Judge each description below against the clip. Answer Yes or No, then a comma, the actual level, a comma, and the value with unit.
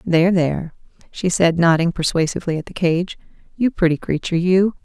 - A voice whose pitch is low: No, medium, 175 Hz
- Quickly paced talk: No, average, 160 wpm